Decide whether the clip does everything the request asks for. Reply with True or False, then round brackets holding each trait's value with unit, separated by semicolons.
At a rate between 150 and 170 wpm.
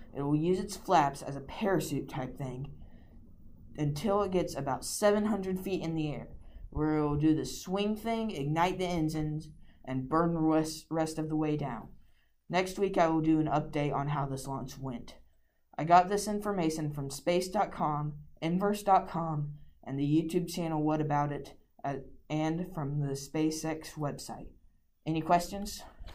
True (165 wpm)